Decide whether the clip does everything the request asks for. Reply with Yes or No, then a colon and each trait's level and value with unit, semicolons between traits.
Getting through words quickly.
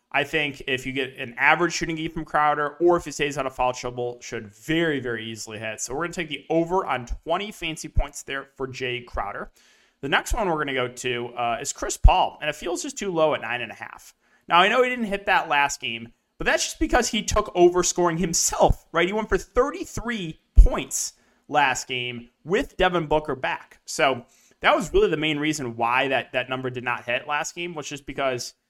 Yes: fast, 230 wpm